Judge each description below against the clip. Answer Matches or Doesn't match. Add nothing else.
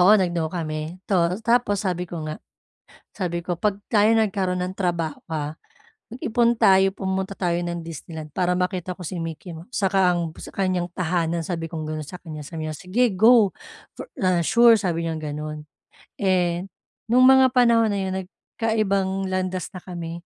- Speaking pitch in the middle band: Matches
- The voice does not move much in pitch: Doesn't match